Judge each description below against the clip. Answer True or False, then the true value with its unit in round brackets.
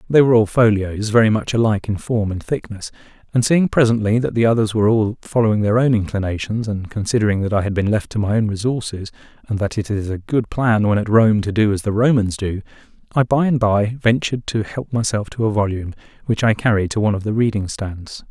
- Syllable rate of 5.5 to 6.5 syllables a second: True (6.0 syllables/s)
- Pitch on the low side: True (110 Hz)